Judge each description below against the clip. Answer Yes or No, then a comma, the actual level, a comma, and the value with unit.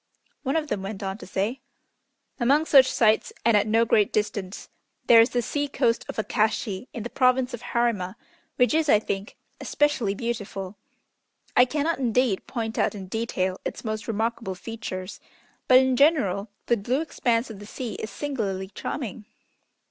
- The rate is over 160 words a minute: Yes, average, 170 wpm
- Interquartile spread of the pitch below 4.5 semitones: Yes, average, 3.8 semitones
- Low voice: No, high, 230 Hz